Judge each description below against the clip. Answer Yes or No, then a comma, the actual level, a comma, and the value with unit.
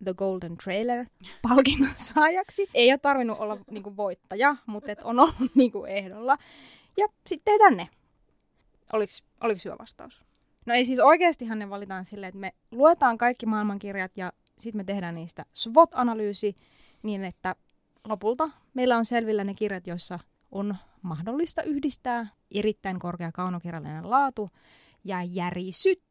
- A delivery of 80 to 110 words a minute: No, average, 140 wpm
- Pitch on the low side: No, high, 215 Hz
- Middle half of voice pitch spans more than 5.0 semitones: Yes, wide, 5.6 semitones